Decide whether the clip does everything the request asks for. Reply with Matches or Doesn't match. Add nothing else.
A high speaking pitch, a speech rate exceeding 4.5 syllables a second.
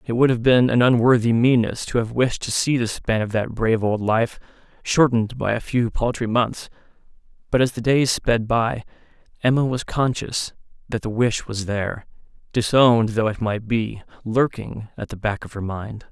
Doesn't match